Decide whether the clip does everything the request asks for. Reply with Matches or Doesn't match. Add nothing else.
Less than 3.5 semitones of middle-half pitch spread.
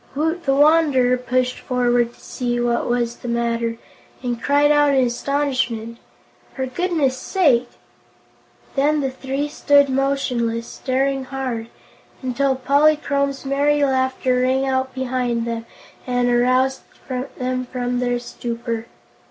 Matches